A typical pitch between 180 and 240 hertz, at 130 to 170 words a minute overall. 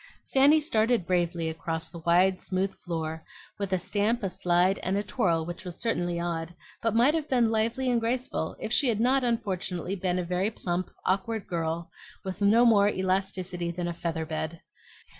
No: medium, 185 Hz; average, 180 wpm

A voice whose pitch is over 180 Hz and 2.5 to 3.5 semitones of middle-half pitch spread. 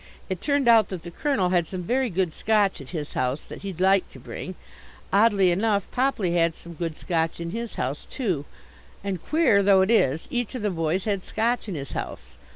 No: high, 190 Hz; average, 4.7 semitones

